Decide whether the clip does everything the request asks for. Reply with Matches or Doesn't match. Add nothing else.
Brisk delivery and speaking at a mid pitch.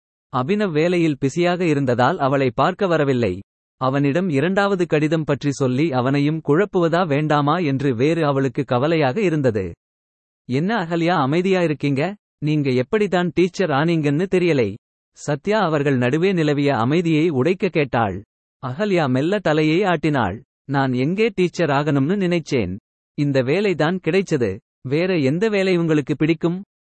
Doesn't match